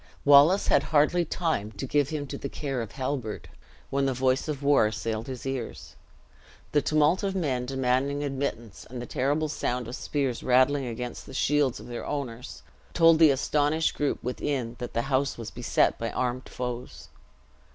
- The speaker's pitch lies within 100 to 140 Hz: Yes, low, 135 Hz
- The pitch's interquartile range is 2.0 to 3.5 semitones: Yes, average, 2.8 semitones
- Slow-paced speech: No, average, 175 wpm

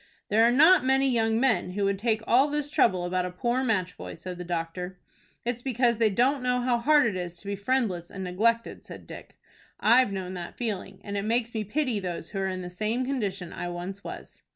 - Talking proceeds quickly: Yes, fast, 225 wpm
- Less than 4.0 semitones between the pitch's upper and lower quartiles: No, average, 5.0 semitones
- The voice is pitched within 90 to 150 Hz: No, high, 215 Hz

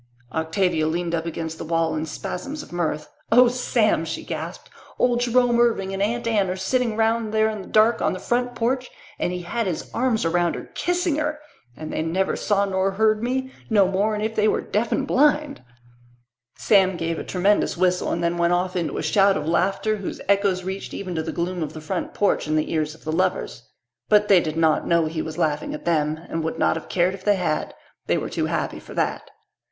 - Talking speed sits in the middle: No, fast, 220 wpm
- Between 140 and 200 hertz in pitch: Yes, high, 190 Hz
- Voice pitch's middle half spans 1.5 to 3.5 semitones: No, average, 4.9 semitones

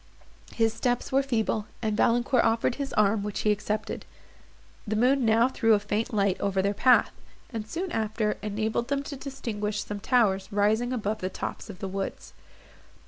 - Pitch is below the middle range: No, high, 220 Hz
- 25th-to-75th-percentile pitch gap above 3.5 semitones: No, average, 2.8 semitones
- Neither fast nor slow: Yes, average, 180 wpm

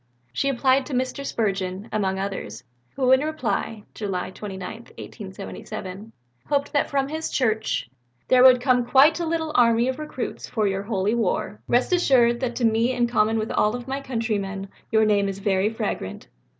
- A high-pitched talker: Yes, high, 230 Hz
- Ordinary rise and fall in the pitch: Yes, average, 4.5 semitones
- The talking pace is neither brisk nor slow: Yes, average, 175 wpm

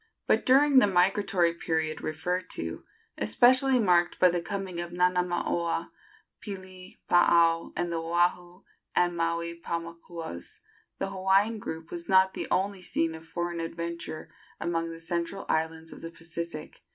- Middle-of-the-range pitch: Yes, medium, 175 Hz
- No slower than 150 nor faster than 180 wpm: No, average, 140 wpm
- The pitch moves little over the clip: Yes, narrow, 2.0 semitones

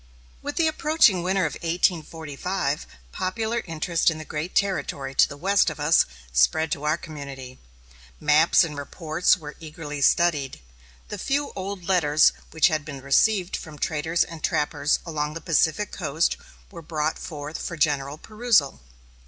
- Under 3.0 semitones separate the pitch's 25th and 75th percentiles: No, average, 3.5 semitones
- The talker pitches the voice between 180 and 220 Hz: No, medium, 160 Hz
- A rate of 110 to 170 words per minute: Yes, average, 155 wpm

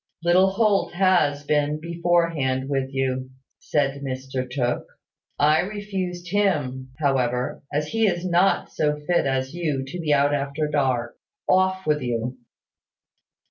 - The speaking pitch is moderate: Yes, medium, 150 Hz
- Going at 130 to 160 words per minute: Yes, slow, 135 wpm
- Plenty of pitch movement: No, average, 4.7 semitones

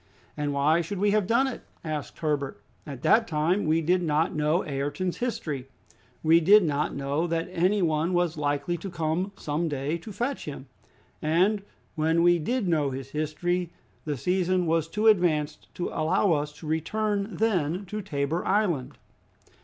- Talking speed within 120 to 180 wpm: Yes, average, 170 wpm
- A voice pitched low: No, medium, 165 Hz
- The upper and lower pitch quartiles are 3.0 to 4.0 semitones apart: Yes, average, 3.7 semitones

